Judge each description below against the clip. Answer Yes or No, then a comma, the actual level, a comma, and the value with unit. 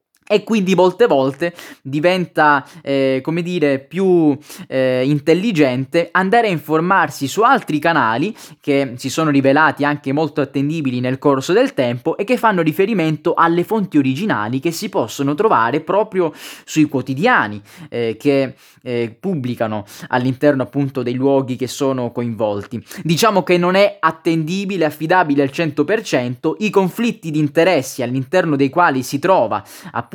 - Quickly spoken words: No, average, 140 wpm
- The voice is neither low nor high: Yes, medium, 150 Hz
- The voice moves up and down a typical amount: Yes, average, 4.8 semitones